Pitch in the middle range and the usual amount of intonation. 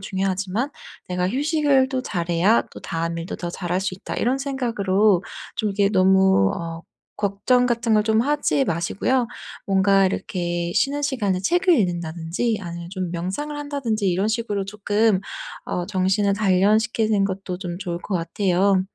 No: high, 195 Hz; average, 4.1 semitones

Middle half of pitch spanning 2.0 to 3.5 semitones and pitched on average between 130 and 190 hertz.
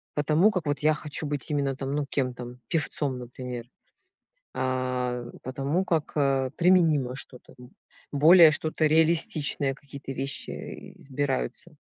Yes: average, 3.2 semitones; medium, 140 Hz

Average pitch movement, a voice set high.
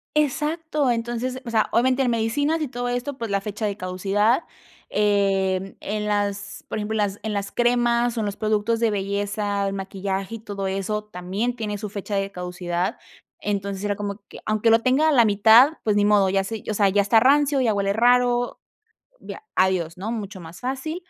Yes: average, 3.3 semitones; high, 210 Hz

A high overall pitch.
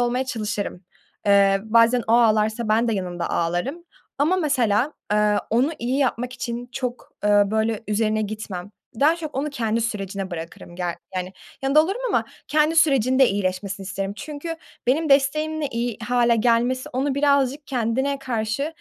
Yes: high, 235 Hz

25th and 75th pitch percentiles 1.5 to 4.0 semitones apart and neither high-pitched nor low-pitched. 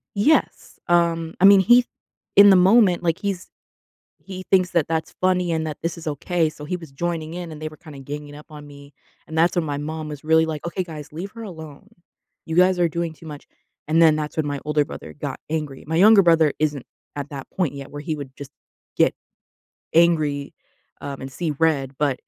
Yes: average, 3.0 semitones; medium, 160 Hz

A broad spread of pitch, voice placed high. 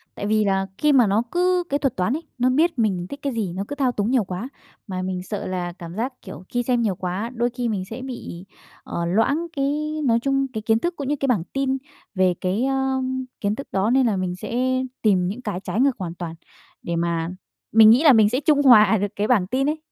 Yes: wide, 5.9 semitones; high, 225 Hz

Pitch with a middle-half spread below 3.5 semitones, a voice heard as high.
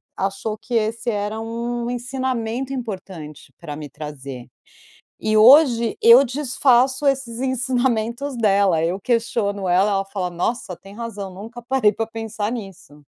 No: average, 3.9 semitones; high, 225 Hz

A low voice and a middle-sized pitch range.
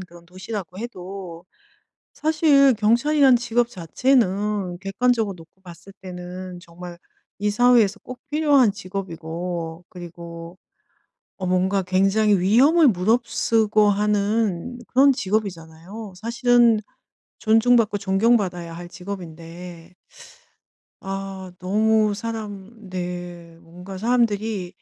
No: high, 195 Hz; average, 4.1 semitones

